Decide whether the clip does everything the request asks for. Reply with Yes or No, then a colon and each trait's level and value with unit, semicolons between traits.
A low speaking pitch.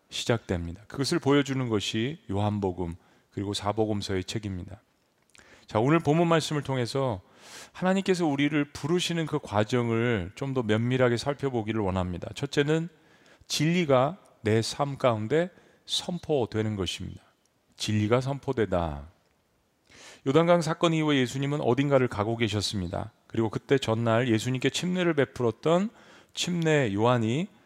Yes: low, 125 Hz